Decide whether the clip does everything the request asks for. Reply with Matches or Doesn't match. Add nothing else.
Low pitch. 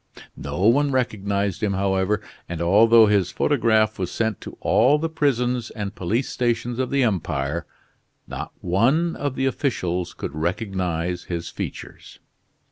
Matches